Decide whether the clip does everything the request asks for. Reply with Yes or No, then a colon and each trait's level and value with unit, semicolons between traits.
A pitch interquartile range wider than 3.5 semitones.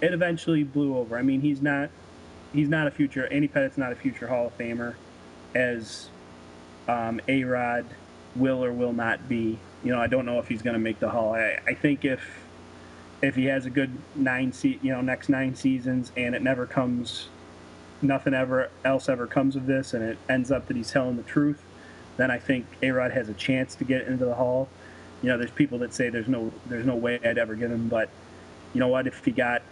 No: average, 3.0 semitones